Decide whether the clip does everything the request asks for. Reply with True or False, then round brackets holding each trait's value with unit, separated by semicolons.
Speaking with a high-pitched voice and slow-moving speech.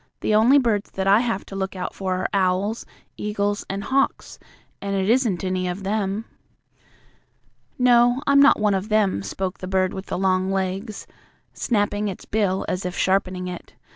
False (195 Hz; 175 wpm)